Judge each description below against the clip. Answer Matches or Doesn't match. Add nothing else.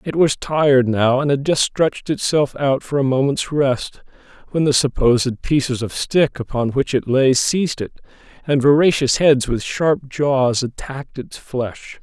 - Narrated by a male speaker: Matches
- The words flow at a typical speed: Matches